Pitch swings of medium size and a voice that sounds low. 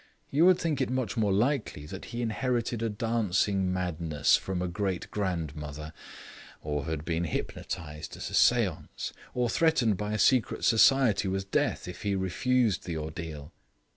No: wide, 6.1 semitones; very low, 95 Hz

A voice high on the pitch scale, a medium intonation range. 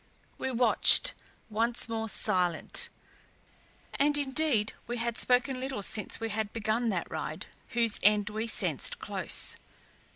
Yes: high, 230 Hz; average, 3.2 semitones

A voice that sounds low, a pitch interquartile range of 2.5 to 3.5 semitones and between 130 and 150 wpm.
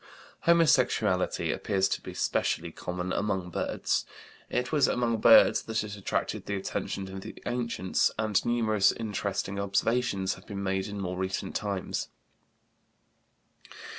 Yes: low, 100 Hz; average, 3.1 semitones; slow, 135 wpm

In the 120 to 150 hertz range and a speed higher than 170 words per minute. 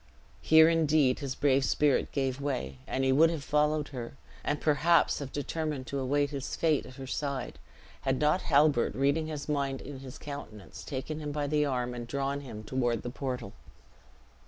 Yes: medium, 140 Hz; average, 180 wpm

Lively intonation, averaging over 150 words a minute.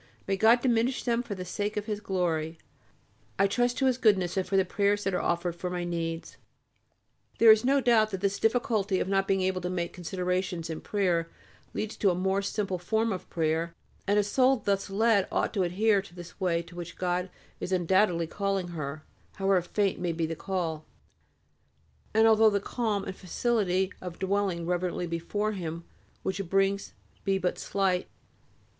No: average, 2.9 semitones; average, 190 wpm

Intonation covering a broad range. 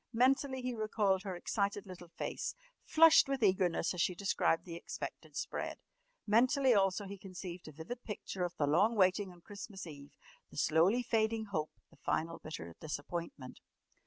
No: average, 4.5 semitones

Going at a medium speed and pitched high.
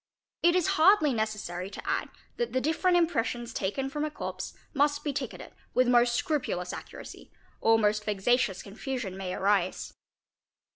Yes: average, 150 wpm; high, 245 Hz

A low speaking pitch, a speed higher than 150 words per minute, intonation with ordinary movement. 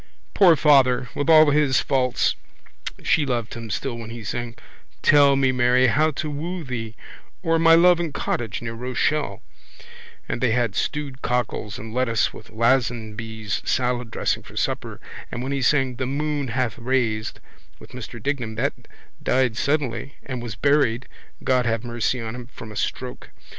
Yes: low, 125 Hz; average, 165 wpm; average, 3.5 semitones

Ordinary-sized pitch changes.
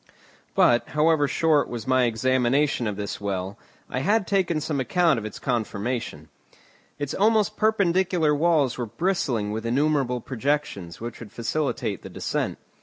No: wide, 5.7 semitones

